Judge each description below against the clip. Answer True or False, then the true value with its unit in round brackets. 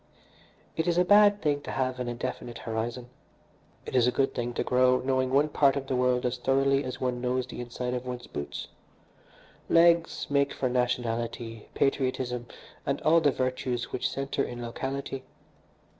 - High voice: False (130 Hz)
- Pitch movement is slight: True (1.9 semitones)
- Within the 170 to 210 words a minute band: True (175 wpm)